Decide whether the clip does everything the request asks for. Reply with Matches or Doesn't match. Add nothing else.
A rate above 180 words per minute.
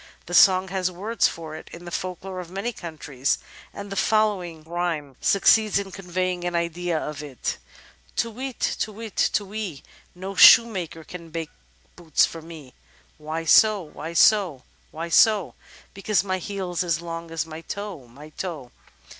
Doesn't match